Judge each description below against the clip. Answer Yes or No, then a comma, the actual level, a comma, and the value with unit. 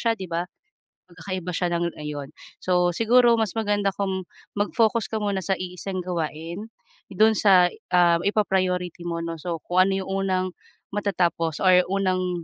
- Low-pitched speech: No, medium, 185 Hz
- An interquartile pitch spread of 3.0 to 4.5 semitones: No, narrow, 2.5 semitones